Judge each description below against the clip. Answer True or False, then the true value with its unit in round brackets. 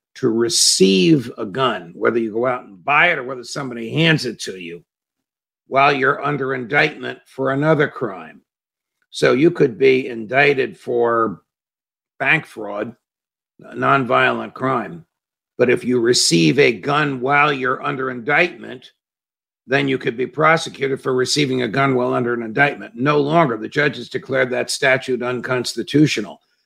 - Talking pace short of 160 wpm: True (150 wpm)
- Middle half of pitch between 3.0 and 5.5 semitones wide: True (3.4 semitones)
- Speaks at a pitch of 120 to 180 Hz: True (135 Hz)